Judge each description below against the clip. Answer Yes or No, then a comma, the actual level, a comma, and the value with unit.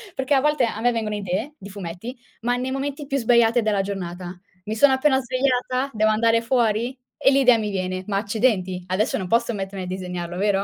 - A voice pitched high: Yes, high, 225 Hz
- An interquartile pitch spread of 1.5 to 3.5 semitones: No, average, 4.8 semitones